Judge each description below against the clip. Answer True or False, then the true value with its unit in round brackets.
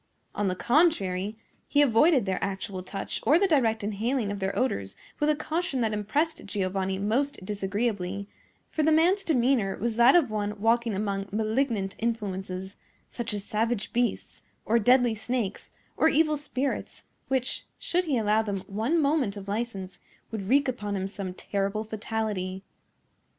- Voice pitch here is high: True (220 Hz)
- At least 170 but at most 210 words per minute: False (155 wpm)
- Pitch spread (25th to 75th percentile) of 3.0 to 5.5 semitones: True (4.9 semitones)